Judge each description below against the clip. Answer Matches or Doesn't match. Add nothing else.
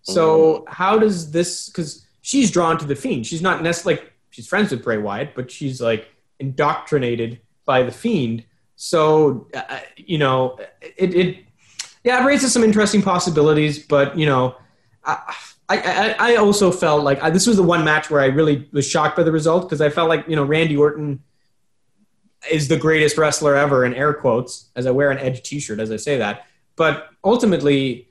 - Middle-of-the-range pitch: Matches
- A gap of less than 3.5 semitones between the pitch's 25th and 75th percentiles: Doesn't match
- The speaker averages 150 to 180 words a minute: Doesn't match